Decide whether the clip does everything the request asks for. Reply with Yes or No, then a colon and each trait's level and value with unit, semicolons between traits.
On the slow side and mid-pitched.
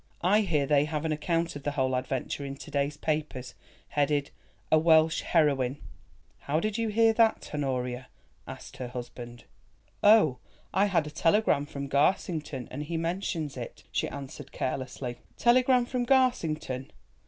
No: average, 155 wpm; medium, 150 Hz